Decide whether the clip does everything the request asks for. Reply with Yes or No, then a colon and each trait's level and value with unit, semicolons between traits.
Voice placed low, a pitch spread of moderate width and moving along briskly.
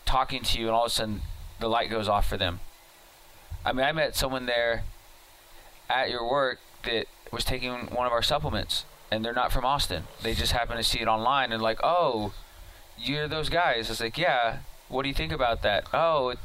Yes: low, 115 Hz; average, 3.2 semitones; fast, 210 wpm